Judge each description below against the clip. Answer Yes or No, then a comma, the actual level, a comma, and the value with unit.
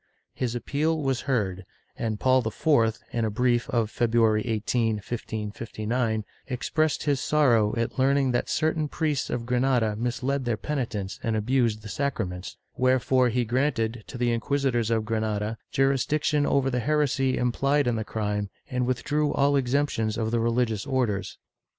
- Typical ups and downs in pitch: Yes, average, 3.5 semitones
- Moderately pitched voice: No, low, 120 Hz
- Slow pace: No, average, 155 wpm